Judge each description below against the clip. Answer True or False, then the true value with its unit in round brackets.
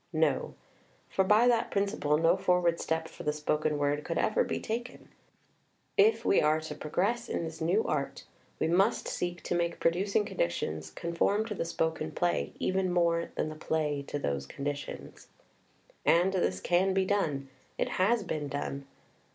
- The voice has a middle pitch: True (170 Hz)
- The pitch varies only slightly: False (4.3 semitones)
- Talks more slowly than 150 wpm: False (170 wpm)